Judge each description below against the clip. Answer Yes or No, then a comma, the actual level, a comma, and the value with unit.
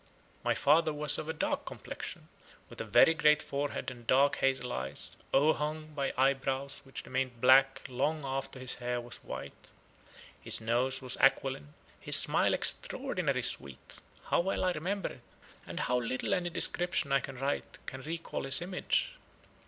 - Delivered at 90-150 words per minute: No, average, 160 wpm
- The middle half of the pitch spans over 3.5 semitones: No, average, 3.1 semitones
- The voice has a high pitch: No, low, 135 Hz